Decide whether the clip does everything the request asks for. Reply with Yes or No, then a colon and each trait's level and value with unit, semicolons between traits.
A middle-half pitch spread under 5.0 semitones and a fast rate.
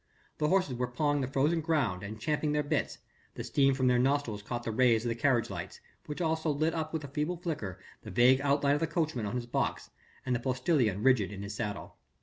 Yes: average, 4.2 semitones; fast, 235 wpm